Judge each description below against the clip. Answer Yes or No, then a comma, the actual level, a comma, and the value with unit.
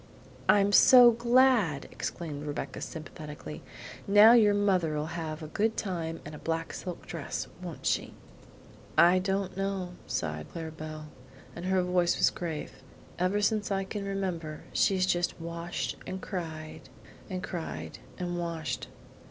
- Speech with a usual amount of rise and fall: Yes, average, 3.7 semitones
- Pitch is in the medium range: Yes, medium, 175 Hz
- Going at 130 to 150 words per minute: Yes, average, 140 wpm